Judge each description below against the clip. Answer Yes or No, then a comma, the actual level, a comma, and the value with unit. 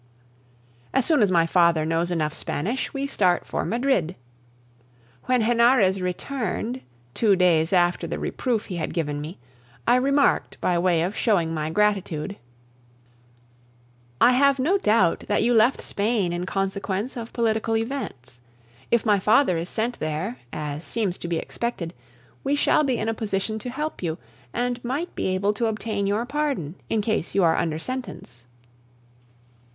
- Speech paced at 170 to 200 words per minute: No, average, 160 wpm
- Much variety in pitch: Yes, wide, 5.9 semitones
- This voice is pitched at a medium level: No, high, 205 Hz